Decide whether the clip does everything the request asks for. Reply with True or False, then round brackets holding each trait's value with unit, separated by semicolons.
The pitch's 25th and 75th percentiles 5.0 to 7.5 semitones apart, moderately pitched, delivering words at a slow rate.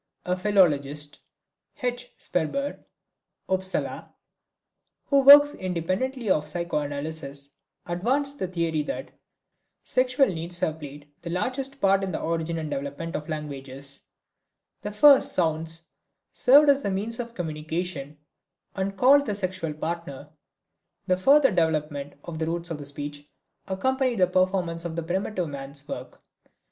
True (5.5 semitones; 170 Hz; 130 wpm)